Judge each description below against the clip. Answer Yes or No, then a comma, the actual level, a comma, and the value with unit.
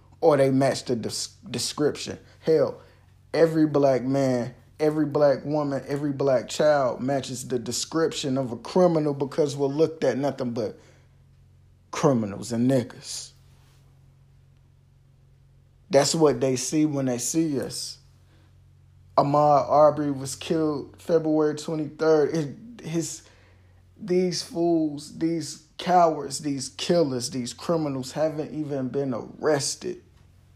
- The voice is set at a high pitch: No, medium, 140 Hz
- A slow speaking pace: Yes, slow, 110 wpm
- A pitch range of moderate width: Yes, average, 3.3 semitones